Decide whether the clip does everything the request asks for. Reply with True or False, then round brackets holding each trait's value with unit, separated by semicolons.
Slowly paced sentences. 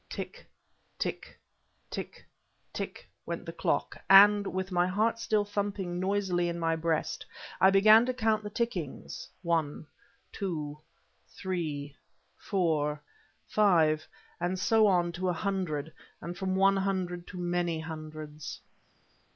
True (125 wpm)